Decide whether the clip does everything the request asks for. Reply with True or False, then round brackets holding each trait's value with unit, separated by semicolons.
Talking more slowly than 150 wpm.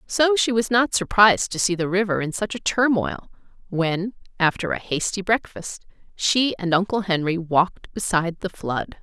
False (175 wpm)